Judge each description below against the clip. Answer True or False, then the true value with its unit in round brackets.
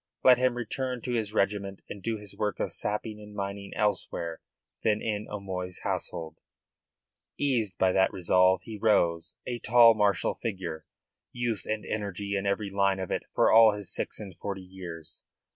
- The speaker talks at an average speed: True (170 wpm)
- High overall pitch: False (100 Hz)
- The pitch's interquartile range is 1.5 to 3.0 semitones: True (2.5 semitones)